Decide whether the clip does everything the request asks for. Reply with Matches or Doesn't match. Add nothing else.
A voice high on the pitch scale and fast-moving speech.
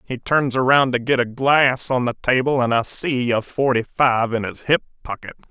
Doesn't match